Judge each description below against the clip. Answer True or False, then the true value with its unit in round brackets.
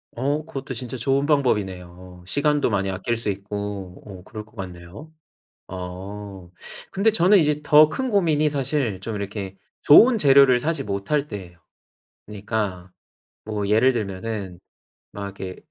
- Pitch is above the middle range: False (110 Hz)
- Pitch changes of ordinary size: False (6.8 semitones)